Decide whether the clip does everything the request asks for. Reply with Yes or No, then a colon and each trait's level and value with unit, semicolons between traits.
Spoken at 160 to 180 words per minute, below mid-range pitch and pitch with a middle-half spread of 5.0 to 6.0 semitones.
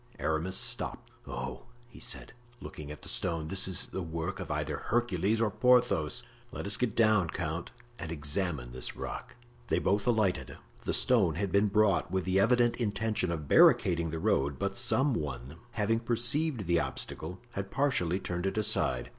Yes: average, 170 wpm; very low, 95 Hz; wide, 5.4 semitones